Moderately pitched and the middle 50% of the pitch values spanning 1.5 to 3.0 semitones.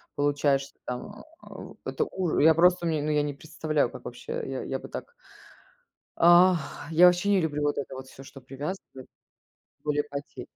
No: medium, 155 Hz; average, 3.7 semitones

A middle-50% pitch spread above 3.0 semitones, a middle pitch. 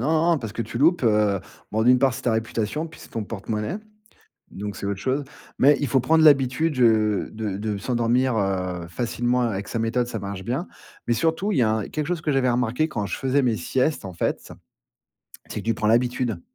No: average, 4.1 semitones; low, 120 Hz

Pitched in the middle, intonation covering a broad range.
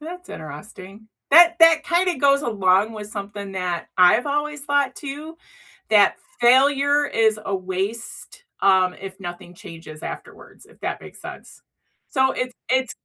No: high, 225 Hz; wide, 7.1 semitones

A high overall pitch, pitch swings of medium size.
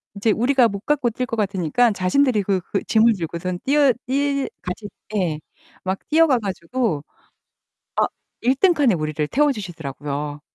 No: high, 210 Hz; wide, 6.8 semitones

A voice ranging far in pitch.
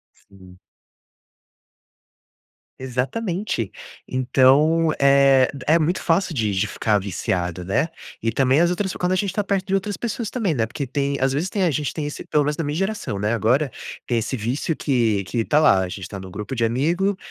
Yes: wide, 7.1 semitones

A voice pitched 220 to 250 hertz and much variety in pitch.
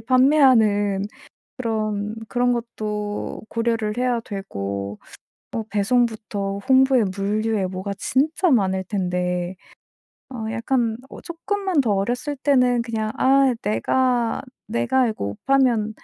No: high, 225 Hz; average, 4.0 semitones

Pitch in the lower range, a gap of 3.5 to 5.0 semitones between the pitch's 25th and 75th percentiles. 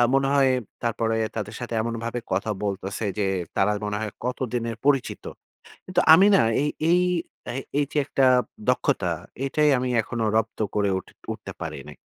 Yes: low, 115 Hz; average, 4.4 semitones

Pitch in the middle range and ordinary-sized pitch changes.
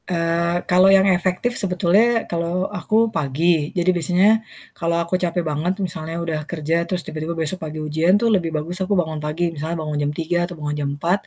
No: medium, 170 Hz; narrow, 2.3 semitones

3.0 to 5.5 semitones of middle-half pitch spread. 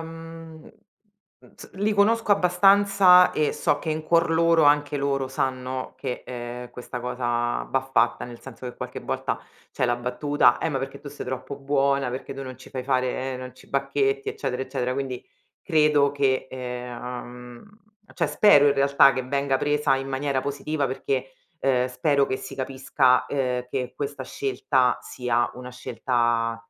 No: narrow, 2.6 semitones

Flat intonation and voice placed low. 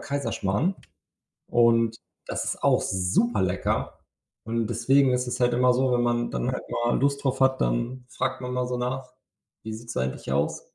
Yes: narrow, 2.3 semitones; low, 120 Hz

